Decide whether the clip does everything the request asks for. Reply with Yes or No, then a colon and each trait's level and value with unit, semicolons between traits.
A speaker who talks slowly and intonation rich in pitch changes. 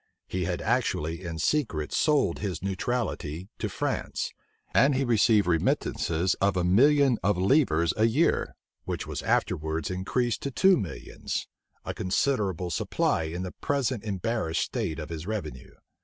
No: average, 145 wpm; wide, 6.5 semitones